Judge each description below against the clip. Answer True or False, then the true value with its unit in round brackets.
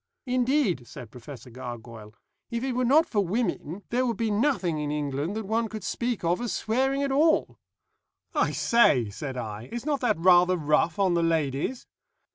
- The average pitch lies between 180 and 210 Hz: True (185 Hz)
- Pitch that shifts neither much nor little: False (8.9 semitones)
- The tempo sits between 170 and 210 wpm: True (180 wpm)